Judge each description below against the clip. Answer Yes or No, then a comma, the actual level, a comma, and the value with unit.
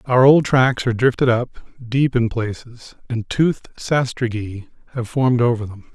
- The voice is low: Yes, low, 120 Hz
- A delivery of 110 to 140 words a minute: No, average, 160 wpm